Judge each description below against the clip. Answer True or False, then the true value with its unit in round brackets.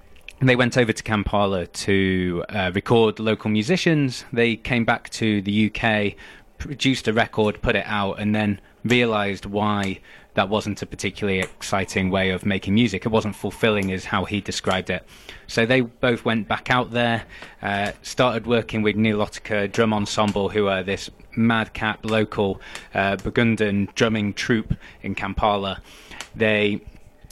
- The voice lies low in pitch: True (105 Hz)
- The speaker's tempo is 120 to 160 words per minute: True (155 wpm)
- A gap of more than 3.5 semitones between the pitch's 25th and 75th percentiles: False (2.5 semitones)